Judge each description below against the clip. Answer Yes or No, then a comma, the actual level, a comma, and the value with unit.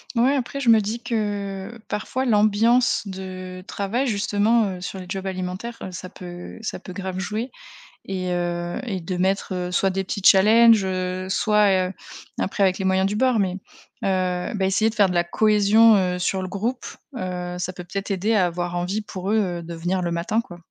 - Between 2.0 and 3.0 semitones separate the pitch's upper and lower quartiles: Yes, average, 2.7 semitones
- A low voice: No, high, 190 Hz